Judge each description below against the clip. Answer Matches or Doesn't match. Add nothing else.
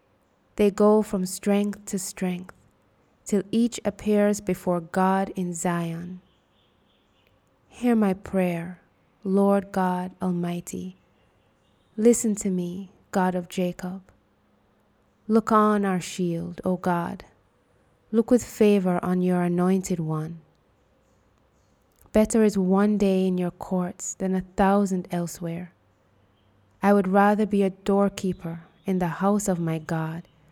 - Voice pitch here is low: Doesn't match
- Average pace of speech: Doesn't match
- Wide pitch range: Doesn't match